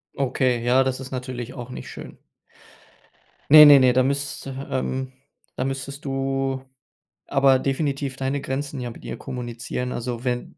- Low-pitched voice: Yes, low, 130 Hz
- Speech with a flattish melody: Yes, narrow, 1.4 semitones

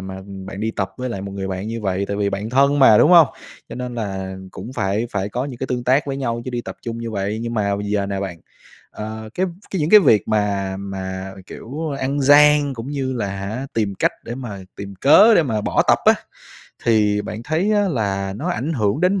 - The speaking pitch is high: No, low, 115 Hz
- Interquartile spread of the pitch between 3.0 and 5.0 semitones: No, wide, 5.5 semitones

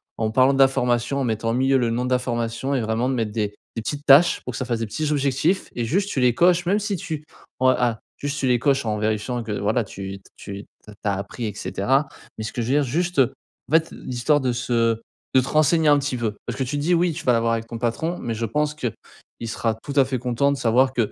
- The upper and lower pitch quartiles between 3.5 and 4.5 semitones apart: Yes, average, 3.8 semitones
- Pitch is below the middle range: Yes, low, 125 Hz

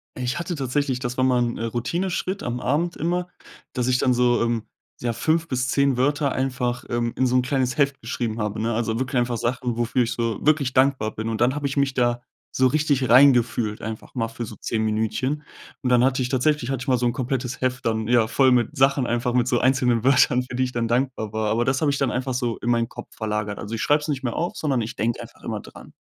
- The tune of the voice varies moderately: No, narrow, 2.3 semitones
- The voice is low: Yes, low, 125 Hz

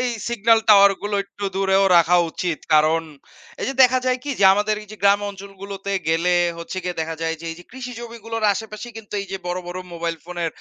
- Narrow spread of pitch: No, average, 3.8 semitones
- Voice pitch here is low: No, high, 195 Hz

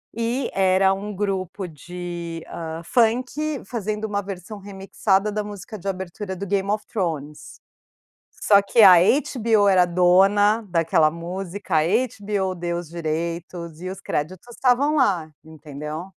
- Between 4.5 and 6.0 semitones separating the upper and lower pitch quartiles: No, average, 3.4 semitones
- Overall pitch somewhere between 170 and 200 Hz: Yes, high, 190 Hz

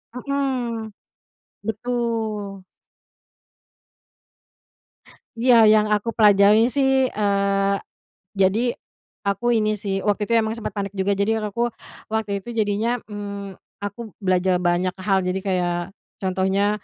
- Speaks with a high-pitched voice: Yes, high, 210 Hz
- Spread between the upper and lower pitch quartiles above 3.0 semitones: No, narrow, 2.5 semitones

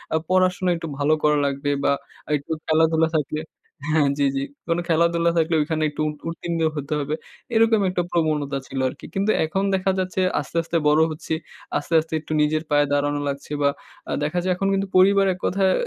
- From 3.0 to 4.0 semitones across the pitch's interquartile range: Yes, average, 3.6 semitones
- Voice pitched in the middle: Yes, medium, 160 Hz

